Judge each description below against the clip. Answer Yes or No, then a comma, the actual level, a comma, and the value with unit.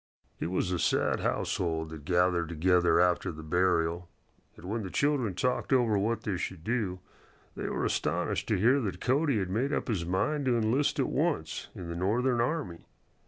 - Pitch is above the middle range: No, very low, 95 Hz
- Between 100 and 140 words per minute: No, average, 185 wpm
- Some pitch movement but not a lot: No, wide, 6.0 semitones